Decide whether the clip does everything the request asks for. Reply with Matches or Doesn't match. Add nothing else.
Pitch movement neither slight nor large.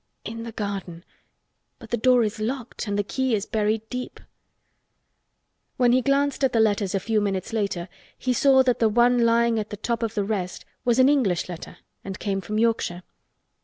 Matches